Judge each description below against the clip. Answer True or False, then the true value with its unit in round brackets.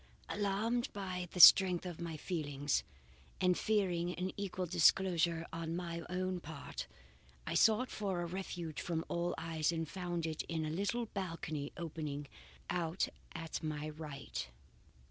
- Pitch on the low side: False (170 Hz)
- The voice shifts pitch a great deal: False (2.6 semitones)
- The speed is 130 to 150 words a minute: True (145 wpm)